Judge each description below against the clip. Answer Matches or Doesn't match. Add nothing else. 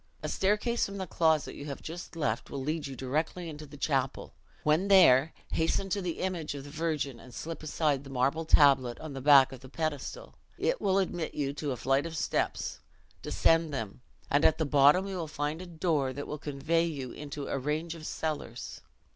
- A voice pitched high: Doesn't match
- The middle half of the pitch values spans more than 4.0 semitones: Doesn't match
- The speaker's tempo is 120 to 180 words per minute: Doesn't match